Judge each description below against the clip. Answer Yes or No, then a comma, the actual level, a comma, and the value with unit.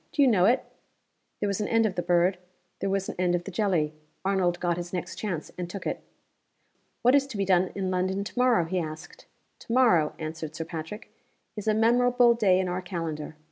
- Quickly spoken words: Yes, fast, 215 wpm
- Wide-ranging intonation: No, average, 3.7 semitones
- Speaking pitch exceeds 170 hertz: Yes, medium, 185 Hz